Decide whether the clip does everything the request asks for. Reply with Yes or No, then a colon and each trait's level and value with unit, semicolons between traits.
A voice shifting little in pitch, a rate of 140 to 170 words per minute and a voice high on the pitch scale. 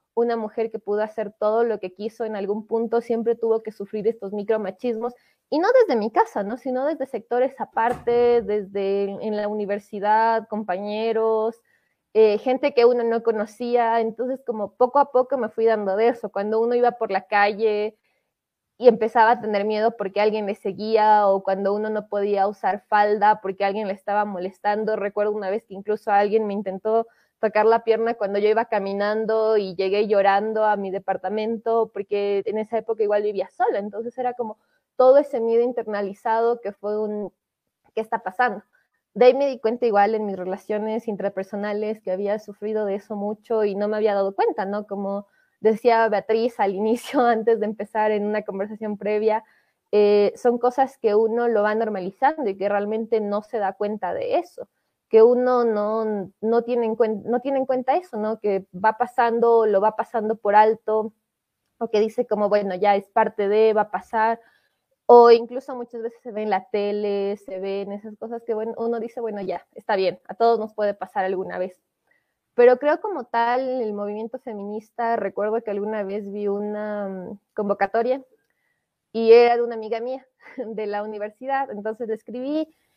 No: narrow, 2.1 semitones; average, 185 wpm; high, 220 Hz